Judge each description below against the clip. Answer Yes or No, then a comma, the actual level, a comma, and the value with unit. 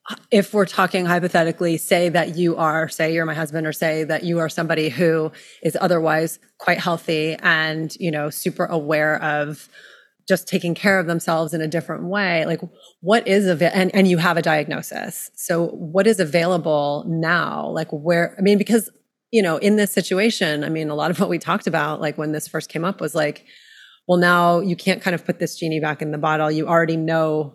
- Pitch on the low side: No, medium, 170 Hz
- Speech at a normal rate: No, fast, 210 wpm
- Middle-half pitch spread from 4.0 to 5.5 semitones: No, average, 2.7 semitones